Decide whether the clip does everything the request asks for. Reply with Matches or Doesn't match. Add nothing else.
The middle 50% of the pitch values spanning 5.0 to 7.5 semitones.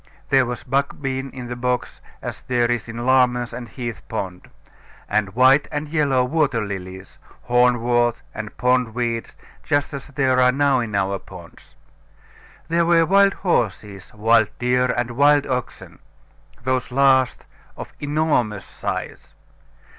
Doesn't match